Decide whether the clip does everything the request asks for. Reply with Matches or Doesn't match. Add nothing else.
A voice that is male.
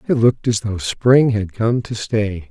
Matches